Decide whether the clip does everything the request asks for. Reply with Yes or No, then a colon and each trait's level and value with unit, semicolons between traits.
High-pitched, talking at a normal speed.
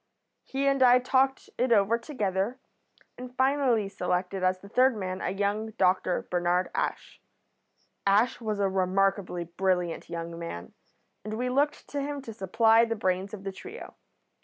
Yes: high, 205 Hz; average, 160 wpm